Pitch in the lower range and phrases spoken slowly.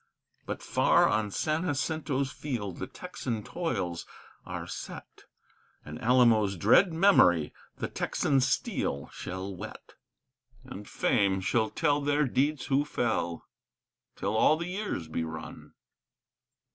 Yes: low, 120 Hz; slow, 120 wpm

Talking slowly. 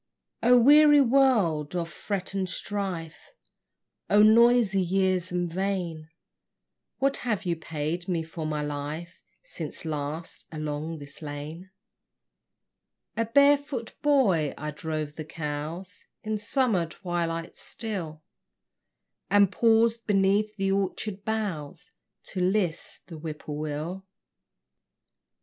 Yes: slow, 110 wpm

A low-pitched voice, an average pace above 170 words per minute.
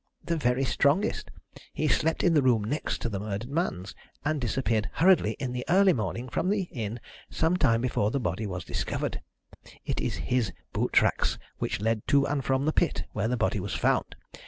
Yes: low, 125 Hz; average, 195 wpm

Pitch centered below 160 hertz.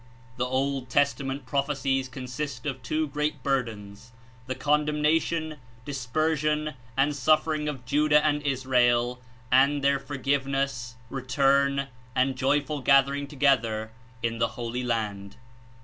Yes: low, 135 Hz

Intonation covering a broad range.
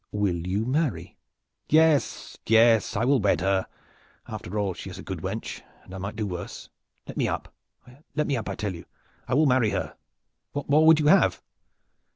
Yes: wide, 6.5 semitones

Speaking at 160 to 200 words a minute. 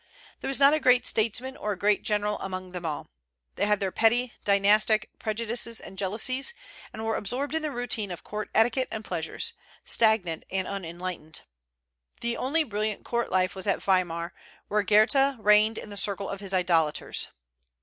Yes: average, 175 wpm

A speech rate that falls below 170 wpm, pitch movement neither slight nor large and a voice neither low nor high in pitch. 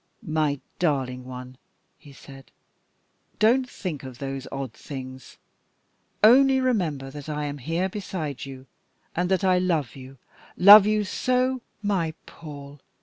No: average, 140 wpm; wide, 6.2 semitones; medium, 155 Hz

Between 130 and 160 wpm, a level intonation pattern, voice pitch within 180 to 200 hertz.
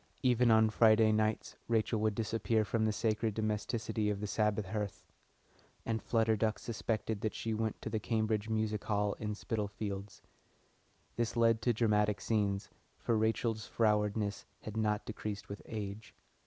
No: average, 155 wpm; narrow, 1.1 semitones; low, 110 Hz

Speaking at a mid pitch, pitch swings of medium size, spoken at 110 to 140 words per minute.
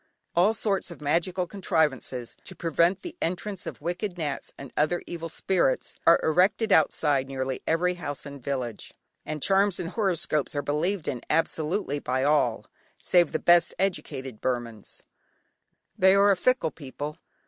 No: medium, 165 Hz; average, 4.5 semitones; average, 150 wpm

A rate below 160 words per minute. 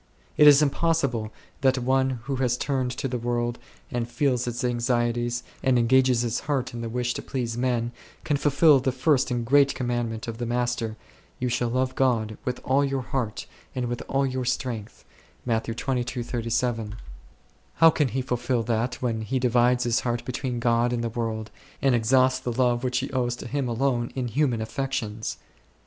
No: average, 180 wpm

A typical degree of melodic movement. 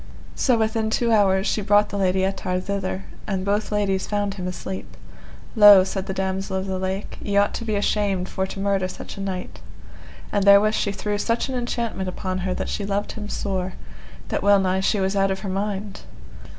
No: narrow, 1.5 semitones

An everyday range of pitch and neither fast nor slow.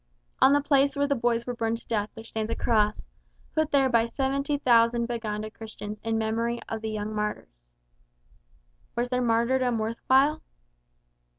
Yes: average, 3.0 semitones; average, 165 wpm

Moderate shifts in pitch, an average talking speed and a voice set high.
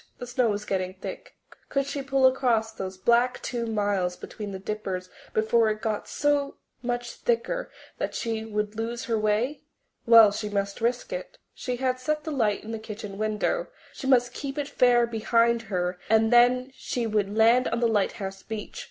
Yes: average, 3.1 semitones; average, 185 wpm; high, 230 Hz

